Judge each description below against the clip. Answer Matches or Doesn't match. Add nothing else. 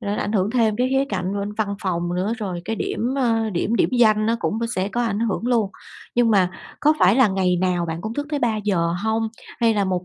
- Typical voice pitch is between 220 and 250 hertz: Doesn't match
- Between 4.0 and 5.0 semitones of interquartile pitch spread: Doesn't match